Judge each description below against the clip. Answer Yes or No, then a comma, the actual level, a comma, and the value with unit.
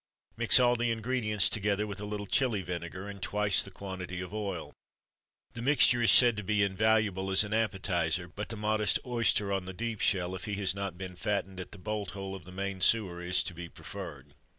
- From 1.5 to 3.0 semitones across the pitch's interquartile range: Yes, narrow, 2.6 semitones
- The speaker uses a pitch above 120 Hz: No, low, 100 Hz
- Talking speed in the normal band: No, fast, 215 wpm